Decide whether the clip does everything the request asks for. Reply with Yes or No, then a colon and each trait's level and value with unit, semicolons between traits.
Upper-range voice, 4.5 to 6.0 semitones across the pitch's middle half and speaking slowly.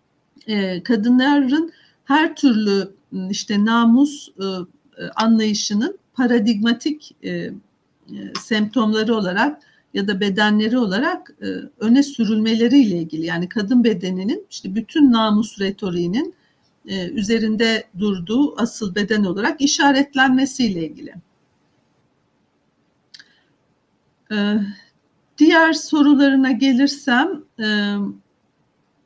Yes: high, 225 Hz; average, 5.2 semitones; slow, 70 wpm